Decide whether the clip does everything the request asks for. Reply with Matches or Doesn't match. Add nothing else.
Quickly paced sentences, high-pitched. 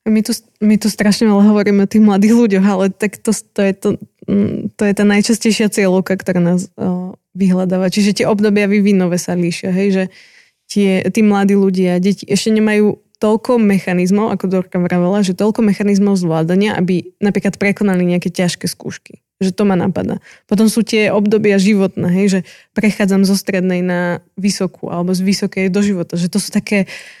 Matches